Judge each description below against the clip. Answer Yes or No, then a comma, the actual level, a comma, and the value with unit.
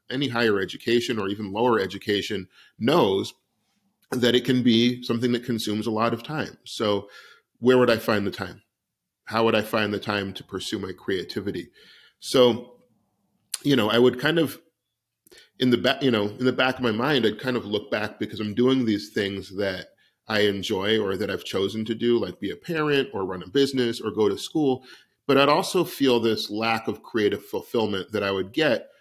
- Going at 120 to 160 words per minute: No, fast, 205 wpm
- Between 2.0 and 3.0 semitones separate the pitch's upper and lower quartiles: No, average, 3.6 semitones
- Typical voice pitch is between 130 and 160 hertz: No, low, 115 Hz